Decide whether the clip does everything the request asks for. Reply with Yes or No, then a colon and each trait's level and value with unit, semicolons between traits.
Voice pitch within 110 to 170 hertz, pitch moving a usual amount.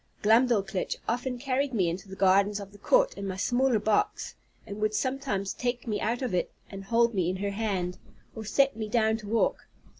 No: high, 215 Hz; average, 3.8 semitones